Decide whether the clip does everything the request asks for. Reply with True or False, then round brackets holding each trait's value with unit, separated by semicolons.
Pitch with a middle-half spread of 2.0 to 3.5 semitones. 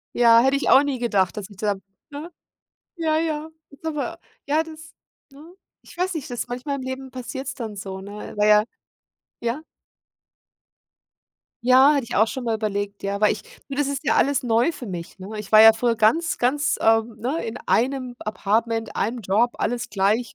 False (4.7 semitones)